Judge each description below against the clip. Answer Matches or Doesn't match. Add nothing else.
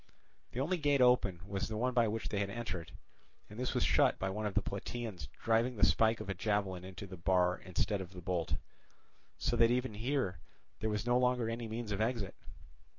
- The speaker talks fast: Matches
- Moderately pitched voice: Doesn't match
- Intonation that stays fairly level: Doesn't match